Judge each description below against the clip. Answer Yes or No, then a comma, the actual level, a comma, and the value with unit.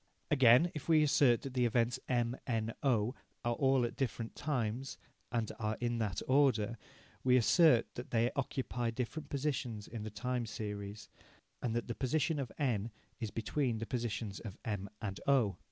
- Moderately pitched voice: No, low, 120 Hz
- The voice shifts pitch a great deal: No, average, 3.2 semitones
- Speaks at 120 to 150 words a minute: No, average, 170 wpm